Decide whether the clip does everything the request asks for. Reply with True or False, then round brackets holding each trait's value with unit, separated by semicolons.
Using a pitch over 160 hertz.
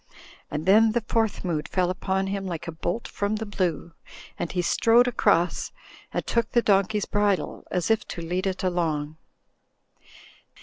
True (190 Hz)